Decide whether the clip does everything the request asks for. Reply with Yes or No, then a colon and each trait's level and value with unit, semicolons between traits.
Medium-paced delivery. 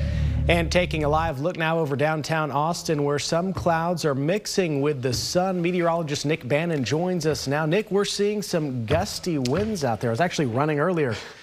Yes: average, 190 wpm